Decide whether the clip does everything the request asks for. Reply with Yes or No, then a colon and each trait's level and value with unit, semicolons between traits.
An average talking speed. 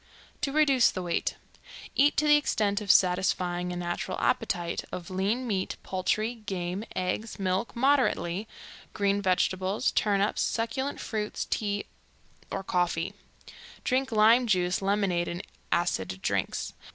No: slow, 125 wpm